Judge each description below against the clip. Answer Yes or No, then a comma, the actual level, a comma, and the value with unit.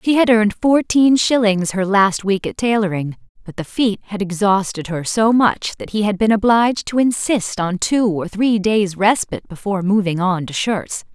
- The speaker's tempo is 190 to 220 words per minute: Yes, average, 195 wpm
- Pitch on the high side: Yes, high, 205 Hz